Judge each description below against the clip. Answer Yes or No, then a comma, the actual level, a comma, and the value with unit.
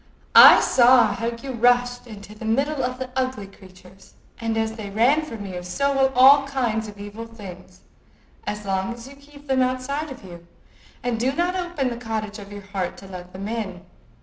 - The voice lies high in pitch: Yes, high, 230 Hz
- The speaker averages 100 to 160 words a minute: No, average, 200 wpm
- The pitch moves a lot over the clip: No, average, 4.5 semitones